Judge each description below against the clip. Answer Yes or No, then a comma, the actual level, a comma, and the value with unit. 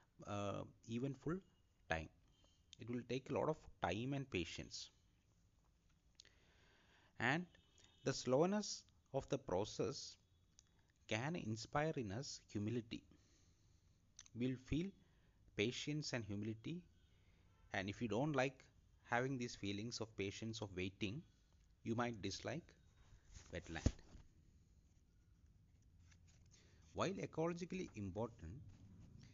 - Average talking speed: No, slow, 100 wpm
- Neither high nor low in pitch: No, low, 100 Hz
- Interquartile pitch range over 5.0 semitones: Yes, wide, 5.5 semitones